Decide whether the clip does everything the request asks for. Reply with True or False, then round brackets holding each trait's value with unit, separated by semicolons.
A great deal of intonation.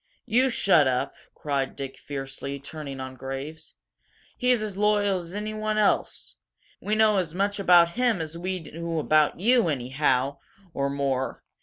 True (6.9 semitones)